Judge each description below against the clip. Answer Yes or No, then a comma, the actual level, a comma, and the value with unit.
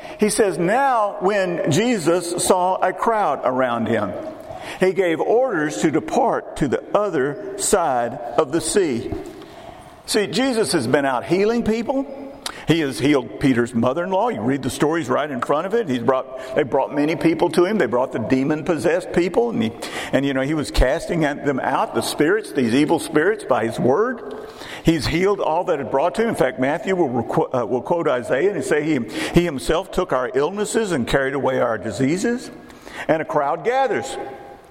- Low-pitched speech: No, medium, 175 Hz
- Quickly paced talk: No, average, 190 wpm